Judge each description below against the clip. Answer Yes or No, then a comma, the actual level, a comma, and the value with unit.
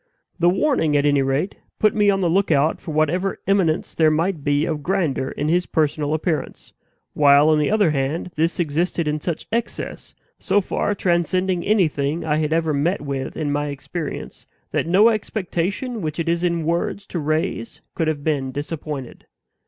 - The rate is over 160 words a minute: Yes, average, 175 wpm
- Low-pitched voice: No, medium, 160 Hz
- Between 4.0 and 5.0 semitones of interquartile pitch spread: No, average, 3.6 semitones